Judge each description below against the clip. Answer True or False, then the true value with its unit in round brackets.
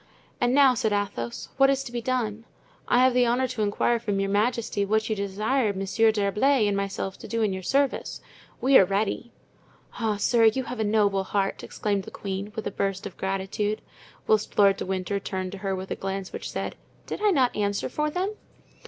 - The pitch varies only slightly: False (3.7 semitones)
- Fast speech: True (210 wpm)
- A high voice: True (210 Hz)